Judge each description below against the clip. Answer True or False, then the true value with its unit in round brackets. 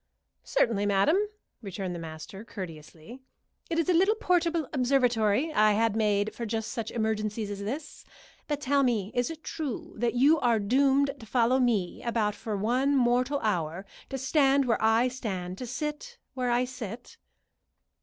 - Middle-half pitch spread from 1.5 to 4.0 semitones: False (4.7 semitones)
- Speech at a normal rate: True (165 wpm)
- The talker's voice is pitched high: True (240 Hz)